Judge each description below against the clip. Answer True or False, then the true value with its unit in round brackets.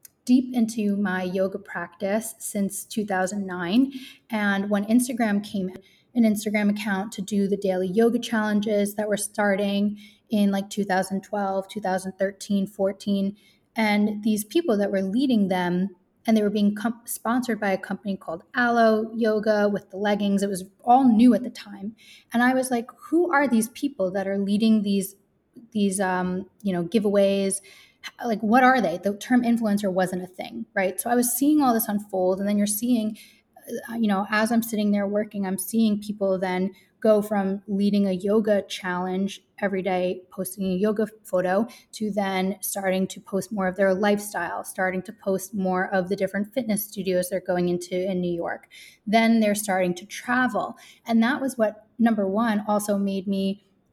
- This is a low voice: False (205 Hz)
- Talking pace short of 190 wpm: True (175 wpm)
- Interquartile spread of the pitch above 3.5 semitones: False (2.4 semitones)